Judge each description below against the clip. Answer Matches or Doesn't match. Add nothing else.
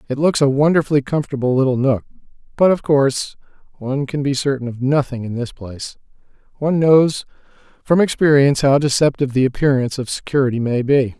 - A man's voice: Matches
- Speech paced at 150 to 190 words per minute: Matches